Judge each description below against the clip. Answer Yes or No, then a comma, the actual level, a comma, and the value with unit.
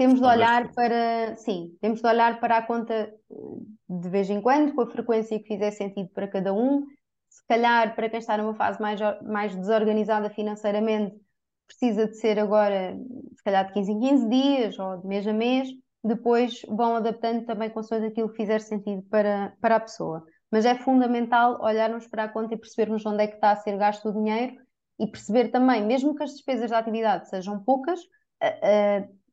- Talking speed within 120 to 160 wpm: No, average, 180 wpm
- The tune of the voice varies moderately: No, narrow, 2.3 semitones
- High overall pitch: Yes, high, 220 Hz